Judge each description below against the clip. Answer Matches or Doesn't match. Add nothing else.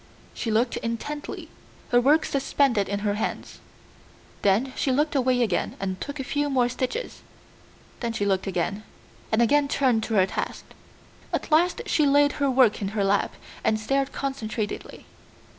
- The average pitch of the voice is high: Matches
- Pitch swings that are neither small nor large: Matches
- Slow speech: Doesn't match